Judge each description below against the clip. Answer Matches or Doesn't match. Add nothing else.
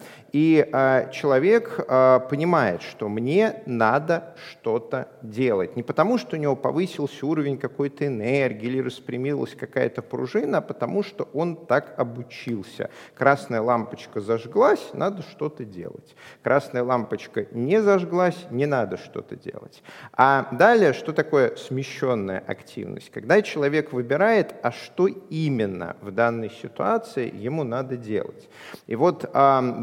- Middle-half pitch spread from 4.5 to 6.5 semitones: Matches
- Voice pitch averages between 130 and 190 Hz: Matches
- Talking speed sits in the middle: Matches